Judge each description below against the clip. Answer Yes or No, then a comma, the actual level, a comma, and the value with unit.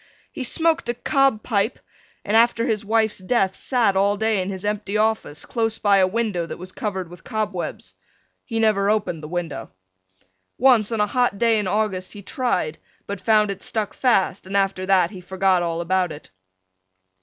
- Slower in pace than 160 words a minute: No, average, 185 wpm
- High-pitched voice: Yes, high, 205 Hz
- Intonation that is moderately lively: Yes, average, 3.2 semitones